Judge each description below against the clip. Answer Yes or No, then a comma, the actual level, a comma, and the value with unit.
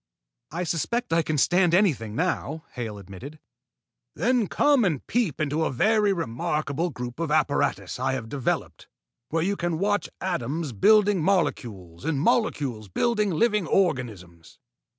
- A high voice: No, medium, 160 Hz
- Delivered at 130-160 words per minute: Yes, average, 140 wpm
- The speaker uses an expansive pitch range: Yes, wide, 7.6 semitones